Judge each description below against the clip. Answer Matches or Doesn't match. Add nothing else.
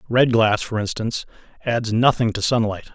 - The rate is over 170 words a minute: Doesn't match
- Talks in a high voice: Doesn't match